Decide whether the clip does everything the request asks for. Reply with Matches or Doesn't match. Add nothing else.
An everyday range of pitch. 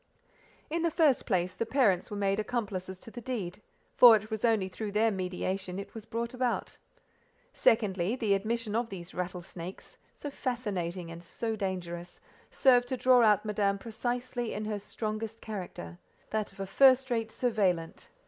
Matches